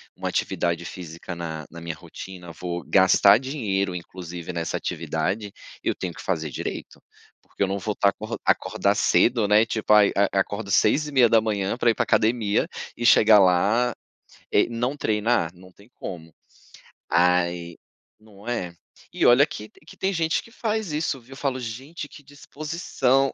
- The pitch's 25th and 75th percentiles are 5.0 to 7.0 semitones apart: Yes, wide, 5.6 semitones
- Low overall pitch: Yes, low, 105 Hz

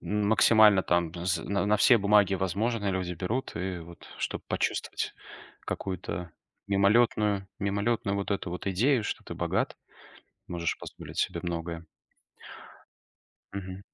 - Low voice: Yes, low, 100 Hz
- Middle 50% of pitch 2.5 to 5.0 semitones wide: Yes, average, 2.9 semitones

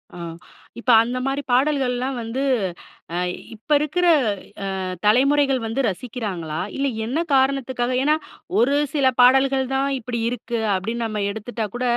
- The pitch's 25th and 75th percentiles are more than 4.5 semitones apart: No, average, 3.1 semitones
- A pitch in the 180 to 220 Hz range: No, very high, 250 Hz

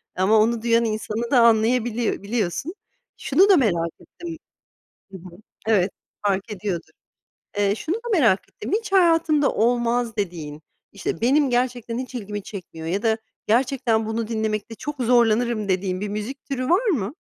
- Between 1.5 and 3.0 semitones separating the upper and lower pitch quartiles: No, average, 3.7 semitones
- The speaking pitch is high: Yes, high, 225 Hz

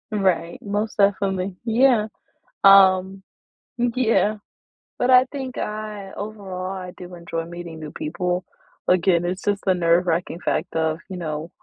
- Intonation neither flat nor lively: Yes, average, 3.3 semitones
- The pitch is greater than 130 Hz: Yes, high, 190 Hz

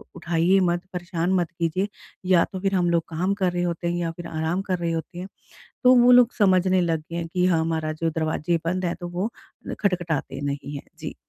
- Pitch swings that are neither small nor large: No, narrow, 2.1 semitones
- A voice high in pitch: No, medium, 175 Hz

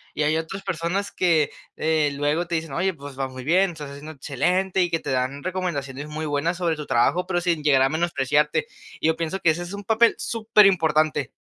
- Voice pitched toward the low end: No, medium, 160 Hz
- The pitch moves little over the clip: No, average, 3.7 semitones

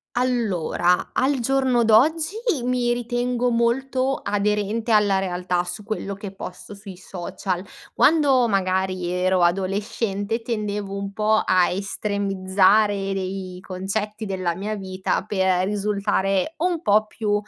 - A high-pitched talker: Yes, high, 205 Hz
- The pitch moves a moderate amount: Yes, average, 3.5 semitones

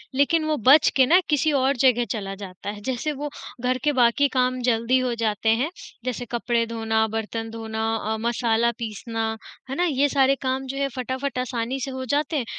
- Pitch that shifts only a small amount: No, average, 3.2 semitones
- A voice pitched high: Yes, very high, 250 Hz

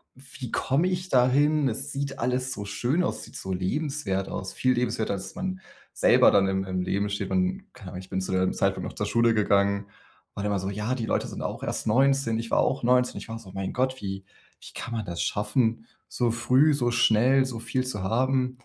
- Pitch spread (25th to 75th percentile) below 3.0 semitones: No, average, 4.8 semitones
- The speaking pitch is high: No, low, 120 Hz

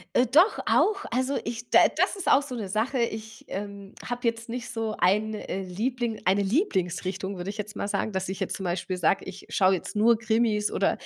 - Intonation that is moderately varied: Yes, average, 3.7 semitones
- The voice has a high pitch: Yes, high, 215 Hz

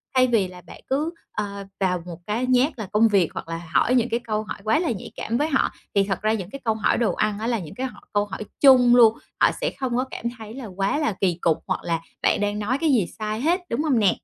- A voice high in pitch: Yes, high, 220 Hz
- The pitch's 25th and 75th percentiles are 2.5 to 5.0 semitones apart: Yes, average, 4.1 semitones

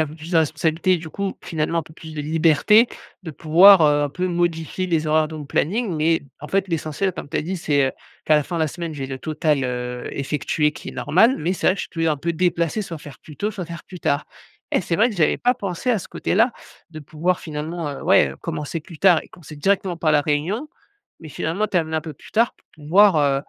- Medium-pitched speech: Yes, medium, 160 Hz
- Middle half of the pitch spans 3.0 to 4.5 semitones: Yes, average, 3.3 semitones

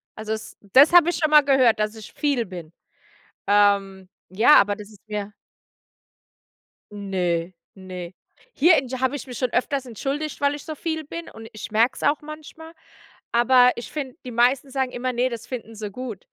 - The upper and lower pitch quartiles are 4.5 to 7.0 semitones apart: Yes, wide, 5.4 semitones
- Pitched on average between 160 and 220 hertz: No, high, 245 Hz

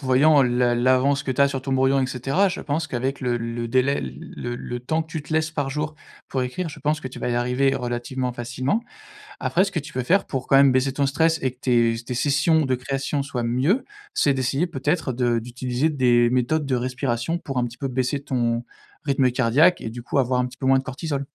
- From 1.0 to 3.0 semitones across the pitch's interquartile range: Yes, narrow, 2.6 semitones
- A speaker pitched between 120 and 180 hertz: Yes, low, 130 Hz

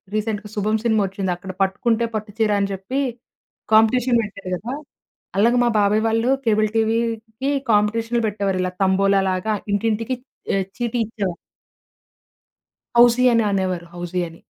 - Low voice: No, high, 215 Hz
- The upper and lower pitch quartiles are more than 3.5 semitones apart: No, average, 2.7 semitones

